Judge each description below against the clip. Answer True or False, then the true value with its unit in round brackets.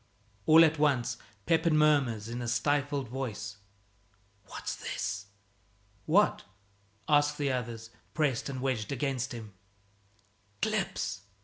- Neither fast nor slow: False (110 wpm)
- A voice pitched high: False (130 Hz)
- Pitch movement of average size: True (4.4 semitones)